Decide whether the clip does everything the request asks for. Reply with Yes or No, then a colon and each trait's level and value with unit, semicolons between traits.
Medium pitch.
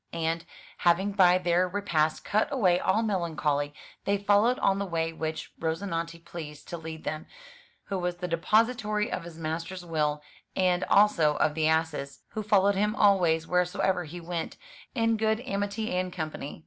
Yes: medium, 175 Hz